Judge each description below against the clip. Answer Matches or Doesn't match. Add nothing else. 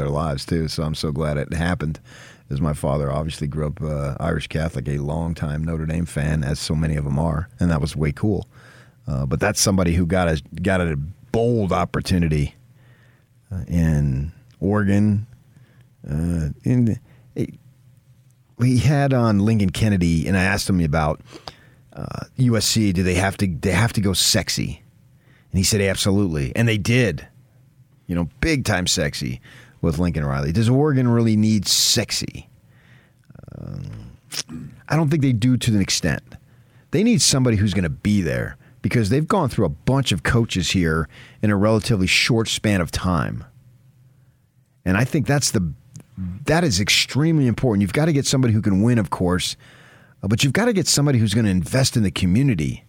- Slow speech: Doesn't match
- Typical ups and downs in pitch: Doesn't match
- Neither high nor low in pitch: Doesn't match